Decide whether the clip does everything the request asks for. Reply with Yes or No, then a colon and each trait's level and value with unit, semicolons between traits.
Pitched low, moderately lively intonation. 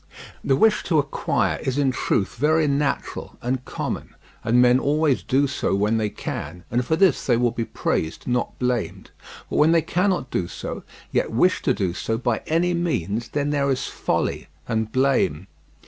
Yes: low, 130 Hz; average, 4.7 semitones